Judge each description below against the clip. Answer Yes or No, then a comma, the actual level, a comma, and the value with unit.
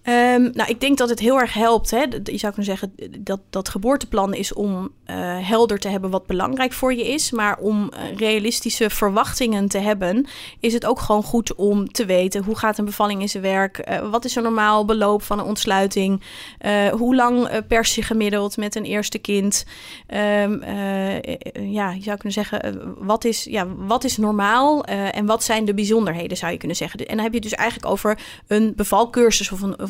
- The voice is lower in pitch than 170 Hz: No, high, 210 Hz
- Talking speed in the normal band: No, fast, 215 wpm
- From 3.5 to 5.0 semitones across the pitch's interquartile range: No, narrow, 2.4 semitones